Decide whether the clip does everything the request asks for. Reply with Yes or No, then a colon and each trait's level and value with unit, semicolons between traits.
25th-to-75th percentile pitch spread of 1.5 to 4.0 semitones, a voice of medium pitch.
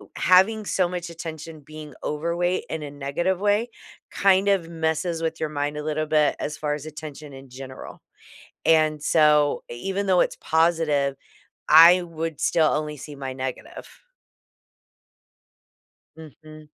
Yes: narrow, 2.5 semitones; medium, 155 Hz